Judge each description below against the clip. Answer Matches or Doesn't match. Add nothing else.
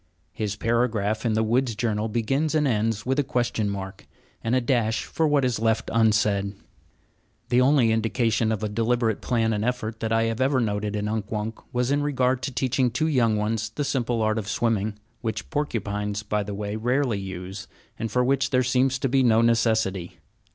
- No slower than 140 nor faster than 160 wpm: Doesn't match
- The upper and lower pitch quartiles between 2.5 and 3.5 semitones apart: Matches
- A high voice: Doesn't match